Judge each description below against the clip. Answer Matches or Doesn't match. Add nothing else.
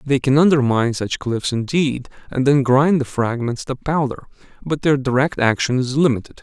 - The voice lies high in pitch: Doesn't match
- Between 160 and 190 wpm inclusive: Matches